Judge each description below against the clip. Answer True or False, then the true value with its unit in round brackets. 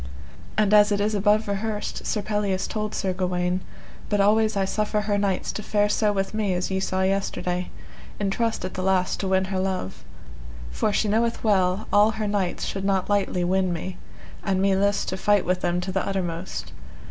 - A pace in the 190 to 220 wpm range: True (200 wpm)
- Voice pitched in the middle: False (195 Hz)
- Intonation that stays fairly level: True (1.9 semitones)